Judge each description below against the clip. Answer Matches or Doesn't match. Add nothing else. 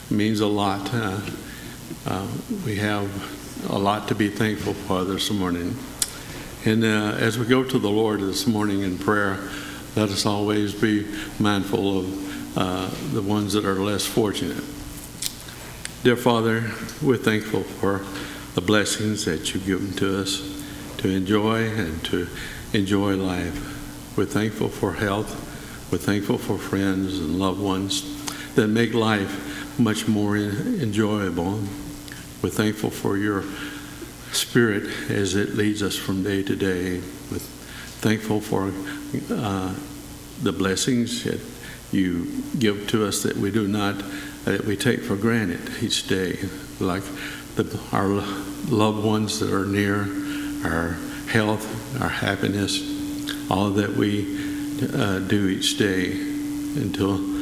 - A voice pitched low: Matches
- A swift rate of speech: Doesn't match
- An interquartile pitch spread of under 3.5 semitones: Matches